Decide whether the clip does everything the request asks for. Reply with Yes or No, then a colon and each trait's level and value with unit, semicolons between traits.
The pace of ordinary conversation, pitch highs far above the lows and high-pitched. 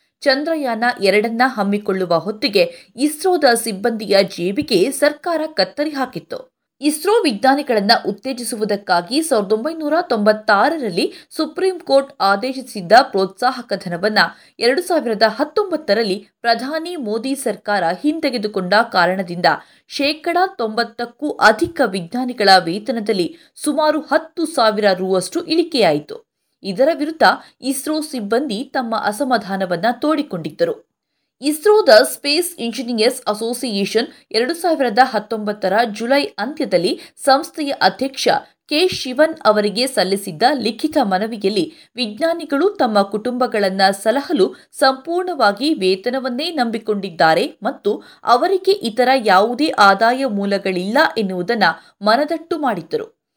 Yes: average, 90 wpm; wide, 6.5 semitones; very high, 250 Hz